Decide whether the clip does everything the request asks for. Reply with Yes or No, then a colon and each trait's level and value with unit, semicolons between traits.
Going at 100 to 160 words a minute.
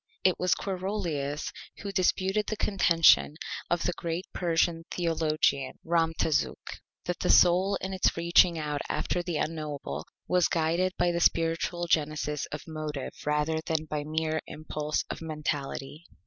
Yes: average, 140 wpm